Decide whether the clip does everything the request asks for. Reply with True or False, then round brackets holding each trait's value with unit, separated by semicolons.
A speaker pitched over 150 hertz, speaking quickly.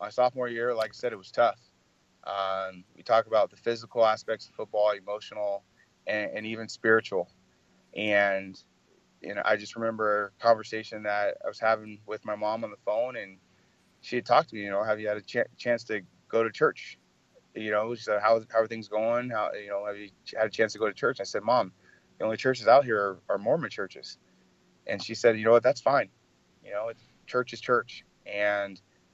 False (110 Hz; 225 wpm)